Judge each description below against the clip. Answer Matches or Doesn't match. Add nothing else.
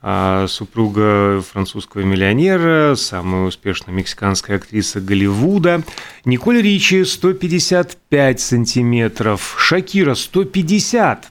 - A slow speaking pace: Matches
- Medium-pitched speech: Doesn't match